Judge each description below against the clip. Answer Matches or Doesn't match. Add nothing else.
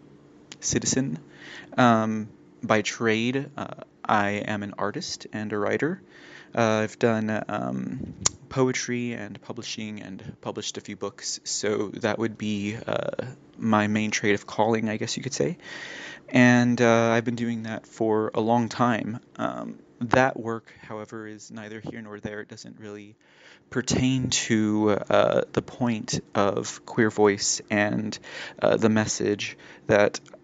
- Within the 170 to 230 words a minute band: Doesn't match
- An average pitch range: Doesn't match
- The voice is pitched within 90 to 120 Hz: Matches